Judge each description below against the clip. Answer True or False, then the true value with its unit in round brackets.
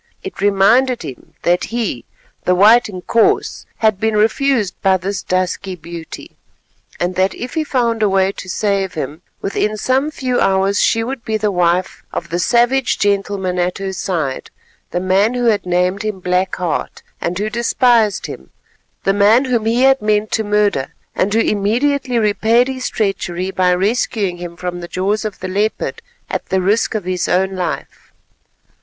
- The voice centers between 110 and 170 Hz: False (200 Hz)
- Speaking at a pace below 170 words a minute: False (175 wpm)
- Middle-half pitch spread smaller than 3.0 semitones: False (3.6 semitones)